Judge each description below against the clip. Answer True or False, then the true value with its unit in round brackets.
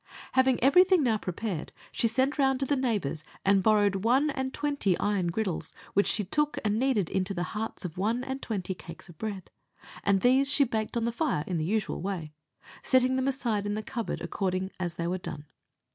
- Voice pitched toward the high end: True (215 Hz)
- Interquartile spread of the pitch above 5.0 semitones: True (5.6 semitones)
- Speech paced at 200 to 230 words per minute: True (205 wpm)